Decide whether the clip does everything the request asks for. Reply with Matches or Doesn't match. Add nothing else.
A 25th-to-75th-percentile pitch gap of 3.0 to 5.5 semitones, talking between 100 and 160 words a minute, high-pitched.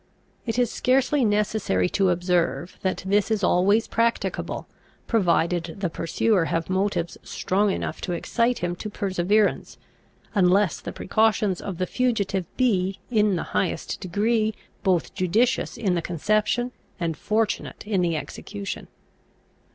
Matches